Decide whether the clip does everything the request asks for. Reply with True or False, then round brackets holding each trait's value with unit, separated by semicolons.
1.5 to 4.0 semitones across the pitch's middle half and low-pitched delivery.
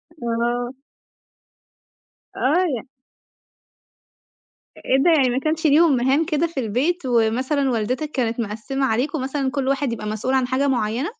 False (3.4 semitones; 265 Hz)